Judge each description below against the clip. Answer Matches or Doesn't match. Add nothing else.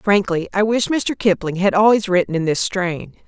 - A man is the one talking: Doesn't match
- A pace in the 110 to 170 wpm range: Doesn't match